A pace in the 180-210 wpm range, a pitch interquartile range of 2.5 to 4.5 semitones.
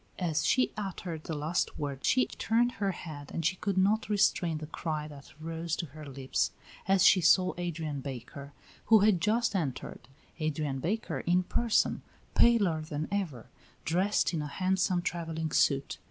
No: average, 165 wpm; average, 4.2 semitones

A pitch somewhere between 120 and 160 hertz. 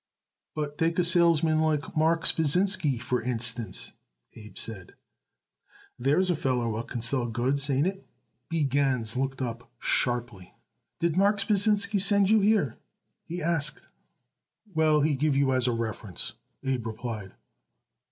Yes: medium, 140 Hz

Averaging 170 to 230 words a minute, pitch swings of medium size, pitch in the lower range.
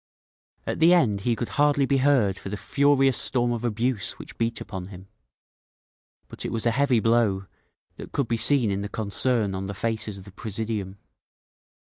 Yes: average, 180 wpm; average, 4.4 semitones; low, 115 Hz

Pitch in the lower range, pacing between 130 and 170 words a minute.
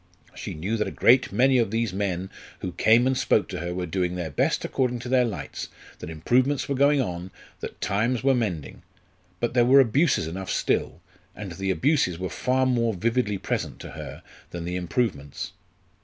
No: low, 110 Hz; average, 190 wpm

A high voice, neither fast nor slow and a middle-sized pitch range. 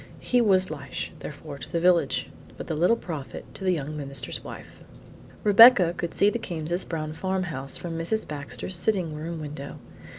No: medium, 165 Hz; average, 170 wpm; average, 3.7 semitones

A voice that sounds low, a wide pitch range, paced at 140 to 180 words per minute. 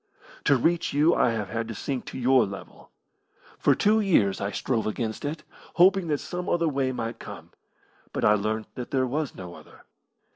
No: low, 130 Hz; wide, 6.1 semitones; average, 190 wpm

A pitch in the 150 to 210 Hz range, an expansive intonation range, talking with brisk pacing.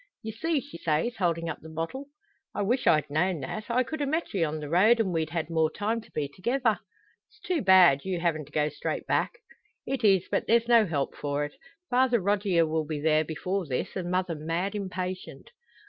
Yes: medium, 185 Hz; wide, 6.0 semitones; fast, 215 wpm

